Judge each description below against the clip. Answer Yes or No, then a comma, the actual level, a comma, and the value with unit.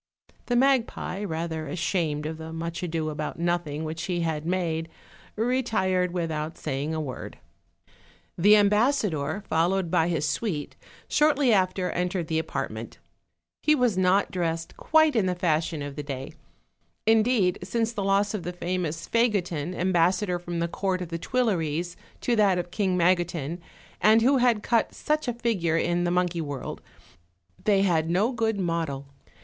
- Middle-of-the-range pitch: Yes, medium, 180 Hz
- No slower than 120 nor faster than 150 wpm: No, average, 160 wpm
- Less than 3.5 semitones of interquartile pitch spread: No, average, 4.3 semitones